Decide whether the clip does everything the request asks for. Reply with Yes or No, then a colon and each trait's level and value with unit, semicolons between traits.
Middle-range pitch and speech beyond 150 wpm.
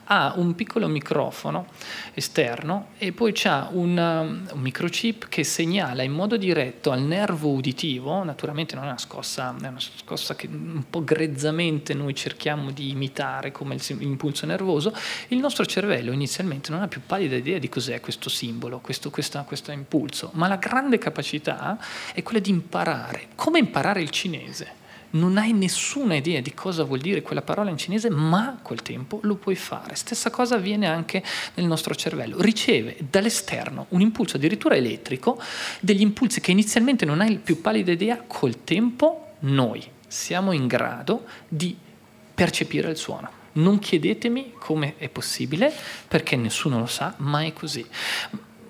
Yes: medium, 170 Hz; average, 160 wpm